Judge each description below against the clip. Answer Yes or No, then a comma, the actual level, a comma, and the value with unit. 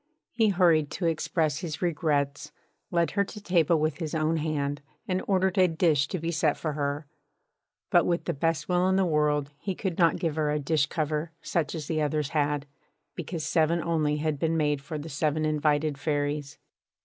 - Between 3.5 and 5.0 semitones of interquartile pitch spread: No, narrow, 2.4 semitones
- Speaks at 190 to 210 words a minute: Yes, average, 195 wpm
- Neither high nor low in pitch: Yes, medium, 155 Hz